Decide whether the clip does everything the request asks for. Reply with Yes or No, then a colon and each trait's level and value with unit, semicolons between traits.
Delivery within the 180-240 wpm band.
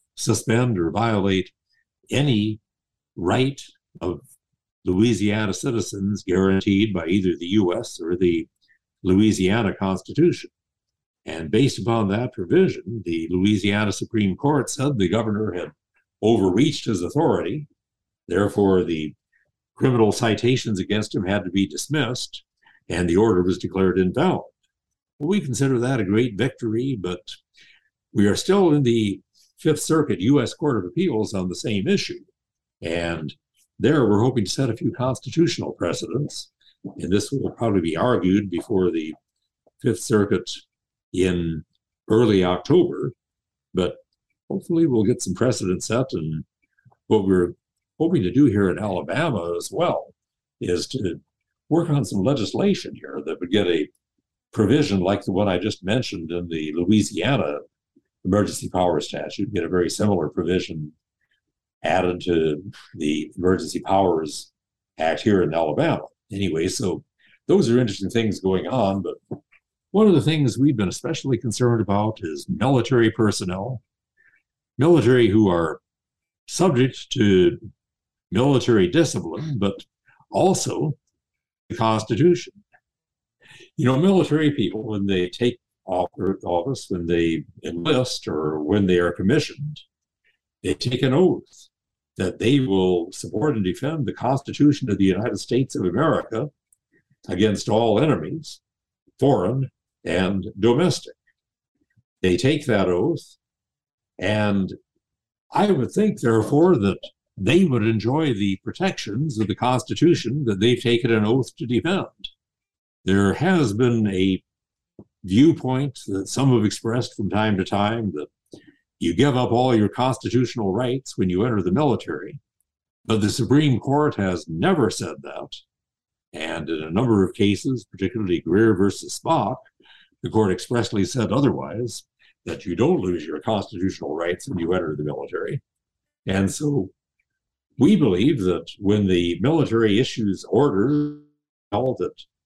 No: slow, 135 wpm